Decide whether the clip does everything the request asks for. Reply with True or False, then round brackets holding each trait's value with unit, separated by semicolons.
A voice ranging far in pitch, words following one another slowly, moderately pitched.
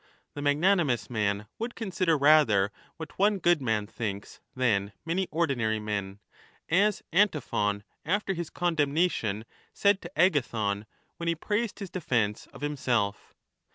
True (8.6 semitones; 130 wpm; 145 Hz)